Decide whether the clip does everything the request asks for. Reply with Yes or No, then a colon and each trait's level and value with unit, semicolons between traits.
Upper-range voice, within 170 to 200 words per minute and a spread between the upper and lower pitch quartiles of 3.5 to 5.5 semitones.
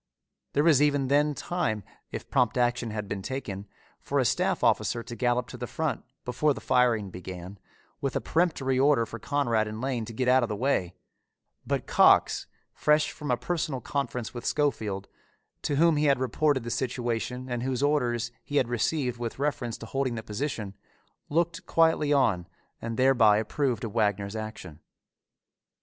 No: low, 125 Hz; average, 175 wpm; average, 4.3 semitones